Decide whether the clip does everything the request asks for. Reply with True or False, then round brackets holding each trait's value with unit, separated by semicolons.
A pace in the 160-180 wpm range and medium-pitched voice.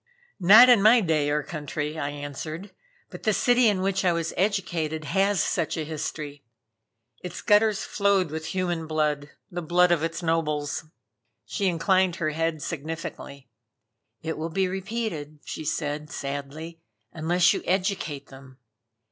False (150 wpm; 165 Hz)